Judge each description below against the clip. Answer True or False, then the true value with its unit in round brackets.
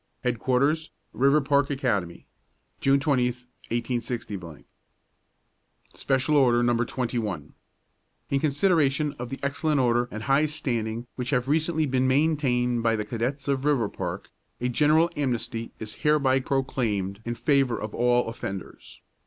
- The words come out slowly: True (125 wpm)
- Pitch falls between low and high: False (130 Hz)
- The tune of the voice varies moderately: True (3.2 semitones)